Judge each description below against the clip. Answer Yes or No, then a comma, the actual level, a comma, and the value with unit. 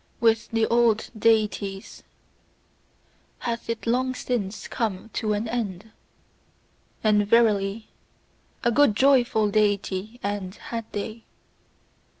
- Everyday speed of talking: No, slow, 105 wpm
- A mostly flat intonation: Yes, narrow, 2.1 semitones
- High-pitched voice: Yes, high, 220 Hz